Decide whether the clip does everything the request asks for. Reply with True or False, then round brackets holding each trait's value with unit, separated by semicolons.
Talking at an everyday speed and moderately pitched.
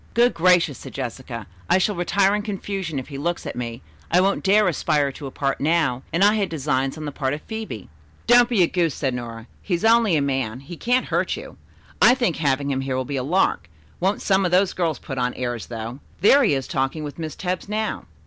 False (235 wpm; 160 Hz)